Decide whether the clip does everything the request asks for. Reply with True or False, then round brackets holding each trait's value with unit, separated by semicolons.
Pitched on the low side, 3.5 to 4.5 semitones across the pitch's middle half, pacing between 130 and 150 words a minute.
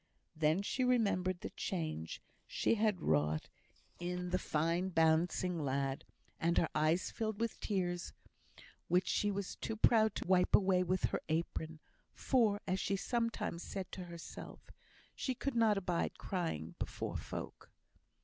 False (180 Hz; 3.9 semitones; 145 wpm)